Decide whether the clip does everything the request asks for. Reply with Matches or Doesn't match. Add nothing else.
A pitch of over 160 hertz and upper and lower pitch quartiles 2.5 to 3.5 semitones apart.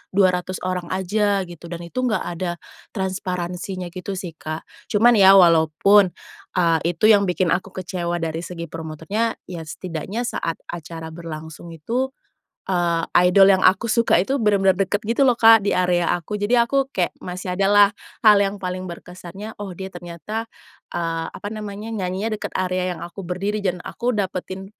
Matches